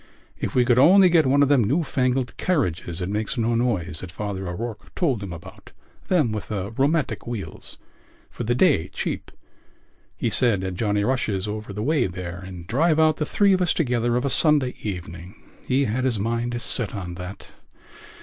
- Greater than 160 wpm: Yes, average, 190 wpm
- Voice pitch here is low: Yes, low, 115 Hz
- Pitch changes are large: Yes, wide, 5.8 semitones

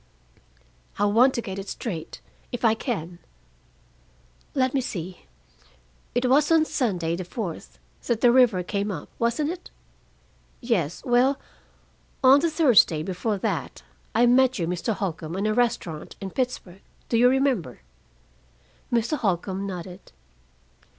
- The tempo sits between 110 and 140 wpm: Yes, slow, 135 wpm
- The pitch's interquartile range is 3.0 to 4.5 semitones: No, wide, 5.6 semitones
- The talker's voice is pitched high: Yes, high, 225 Hz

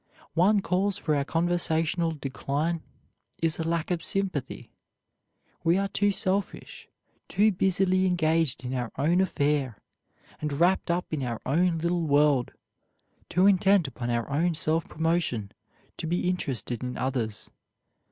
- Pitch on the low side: No, medium, 165 Hz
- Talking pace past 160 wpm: No, average, 140 wpm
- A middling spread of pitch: Yes, average, 4.3 semitones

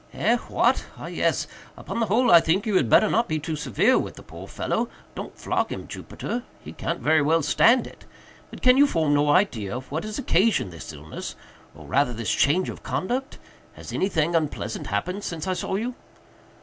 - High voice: No, medium, 170 Hz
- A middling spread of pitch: No, wide, 6.8 semitones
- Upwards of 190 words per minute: No, average, 180 wpm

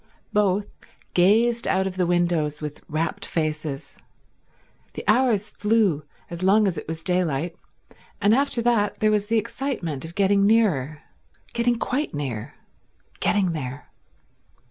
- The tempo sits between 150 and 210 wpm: No, slow, 135 wpm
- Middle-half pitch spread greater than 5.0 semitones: Yes, wide, 5.4 semitones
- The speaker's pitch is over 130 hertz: Yes, high, 190 Hz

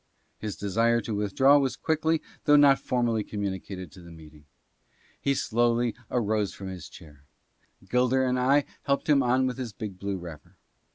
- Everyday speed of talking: Yes, average, 170 wpm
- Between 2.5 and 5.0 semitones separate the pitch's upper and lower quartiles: No, wide, 5.4 semitones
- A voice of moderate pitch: No, low, 115 Hz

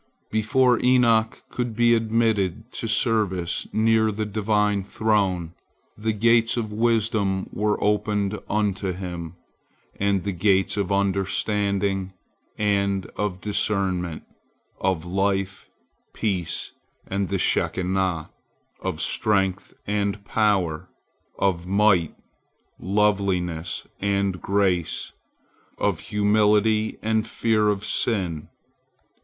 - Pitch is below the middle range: Yes, low, 100 Hz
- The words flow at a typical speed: No, slow, 100 wpm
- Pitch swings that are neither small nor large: No, narrow, 2.2 semitones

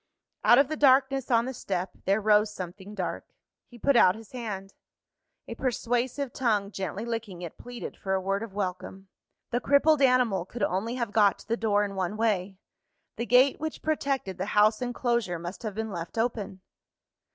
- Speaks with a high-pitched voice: Yes, high, 220 Hz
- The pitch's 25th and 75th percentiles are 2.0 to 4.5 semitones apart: Yes, average, 4.1 semitones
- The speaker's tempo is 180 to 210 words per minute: Yes, average, 185 wpm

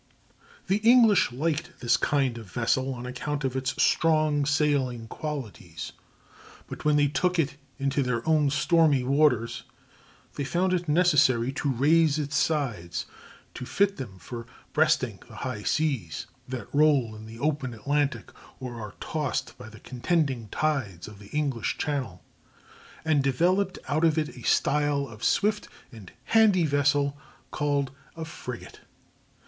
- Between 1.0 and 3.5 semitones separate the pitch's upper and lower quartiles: No, average, 4.2 semitones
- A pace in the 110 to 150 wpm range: Yes, average, 145 wpm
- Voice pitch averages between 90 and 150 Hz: Yes, medium, 140 Hz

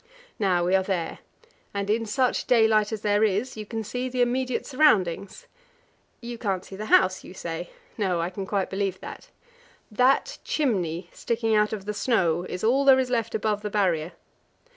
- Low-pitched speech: No, high, 210 Hz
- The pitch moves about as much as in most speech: Yes, average, 4.1 semitones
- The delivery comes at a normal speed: Yes, average, 185 wpm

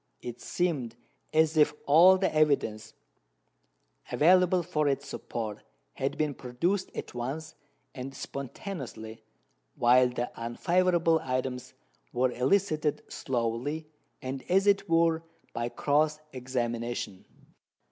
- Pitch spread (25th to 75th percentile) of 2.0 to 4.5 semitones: No, average, 5.1 semitones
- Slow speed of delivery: Yes, slow, 105 wpm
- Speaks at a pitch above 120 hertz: Yes, medium, 140 Hz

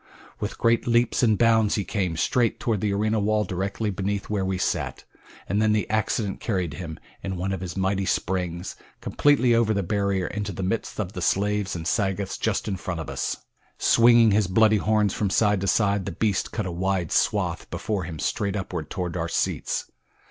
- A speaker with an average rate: Yes, average, 195 wpm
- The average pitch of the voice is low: Yes, low, 100 Hz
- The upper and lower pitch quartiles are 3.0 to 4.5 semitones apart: No, narrow, 2.6 semitones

